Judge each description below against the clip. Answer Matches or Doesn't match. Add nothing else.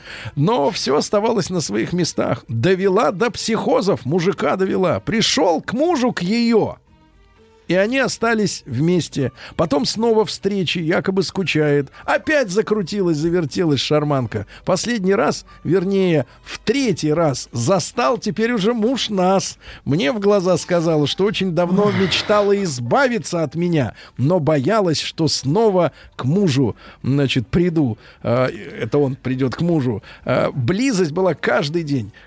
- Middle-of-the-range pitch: Matches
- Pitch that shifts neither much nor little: Doesn't match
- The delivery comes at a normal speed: Matches